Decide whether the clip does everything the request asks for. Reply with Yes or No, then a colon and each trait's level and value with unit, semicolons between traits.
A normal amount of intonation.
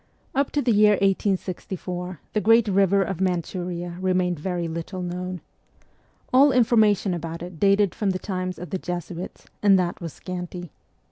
No: narrow, 2.1 semitones